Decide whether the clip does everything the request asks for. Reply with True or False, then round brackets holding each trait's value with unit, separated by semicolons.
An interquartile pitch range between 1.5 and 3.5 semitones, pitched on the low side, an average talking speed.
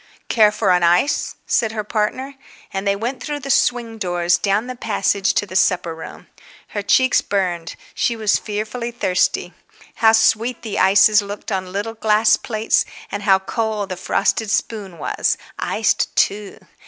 False (2.7 semitones; 210 Hz; 165 wpm)